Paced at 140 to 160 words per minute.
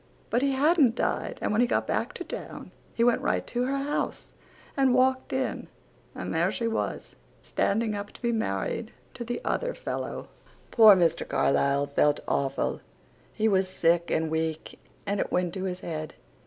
No: average, 180 wpm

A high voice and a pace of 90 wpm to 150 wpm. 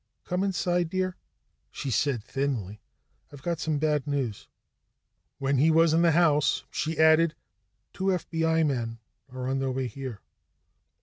No: medium, 150 Hz; average, 145 wpm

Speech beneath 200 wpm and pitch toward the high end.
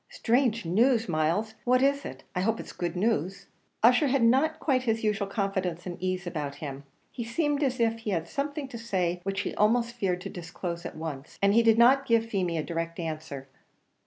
No: fast, 205 wpm; high, 205 Hz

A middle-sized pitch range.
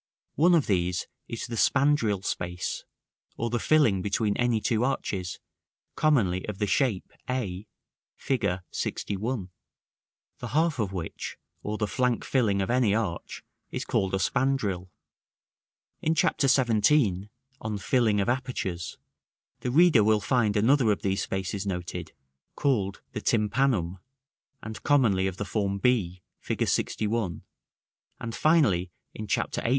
Yes: average, 4.7 semitones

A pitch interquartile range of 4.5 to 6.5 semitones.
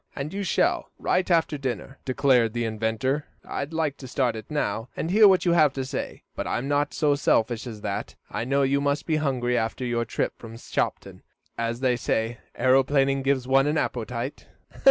No: average, 3.4 semitones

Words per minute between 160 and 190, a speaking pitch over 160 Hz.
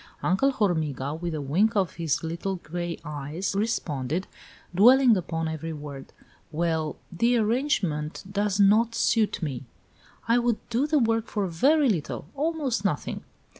No: average, 140 wpm; medium, 185 Hz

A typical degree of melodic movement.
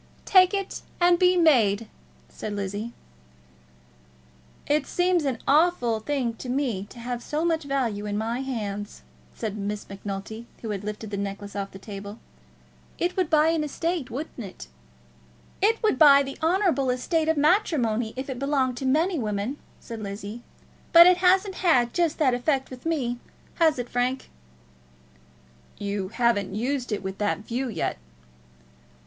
No: wide, 7.0 semitones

